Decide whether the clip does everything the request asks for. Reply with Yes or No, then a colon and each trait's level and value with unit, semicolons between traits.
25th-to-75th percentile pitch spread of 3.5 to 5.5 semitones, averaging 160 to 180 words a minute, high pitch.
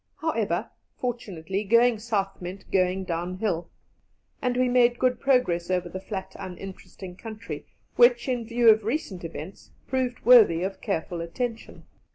No: average, 4.9 semitones; average, 140 wpm; high, 200 Hz